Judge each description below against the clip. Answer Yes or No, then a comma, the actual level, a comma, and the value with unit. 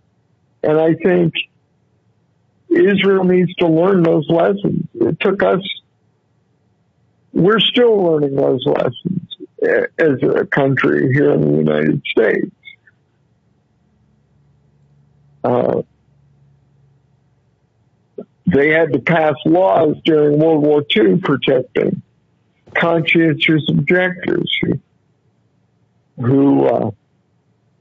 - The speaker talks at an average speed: No, slow, 90 wpm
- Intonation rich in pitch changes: No, average, 4.1 semitones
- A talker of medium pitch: Yes, medium, 155 Hz